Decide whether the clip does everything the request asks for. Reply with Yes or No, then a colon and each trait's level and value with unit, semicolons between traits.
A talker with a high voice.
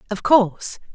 Yes: high, 210 Hz